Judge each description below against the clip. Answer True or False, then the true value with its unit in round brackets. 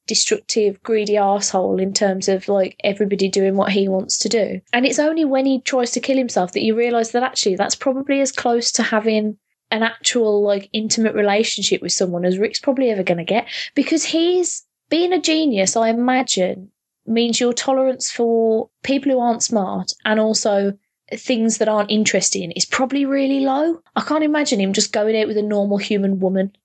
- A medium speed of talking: True (190 wpm)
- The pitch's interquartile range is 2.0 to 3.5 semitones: False (4.3 semitones)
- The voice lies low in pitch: False (220 Hz)